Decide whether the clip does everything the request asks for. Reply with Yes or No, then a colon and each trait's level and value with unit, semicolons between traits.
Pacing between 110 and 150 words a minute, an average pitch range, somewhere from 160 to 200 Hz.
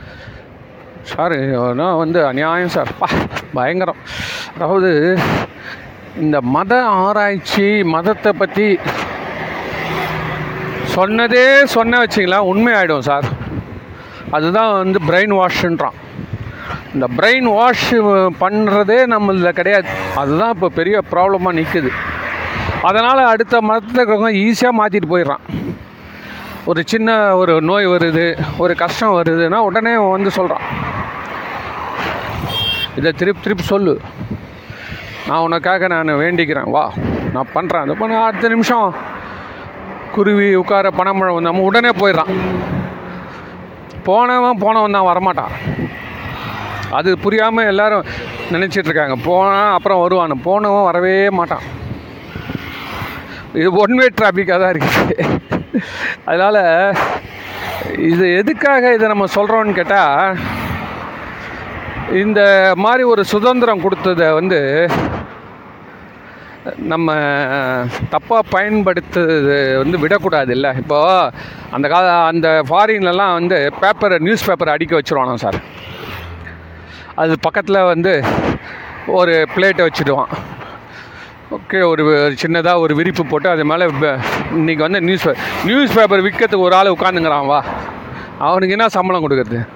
No: average, 100 wpm; average, 4.2 semitones; medium, 185 Hz